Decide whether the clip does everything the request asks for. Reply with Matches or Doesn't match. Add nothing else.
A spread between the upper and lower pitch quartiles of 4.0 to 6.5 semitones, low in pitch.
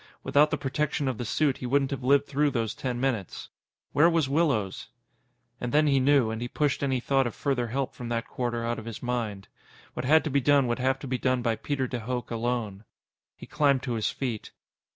Doesn't match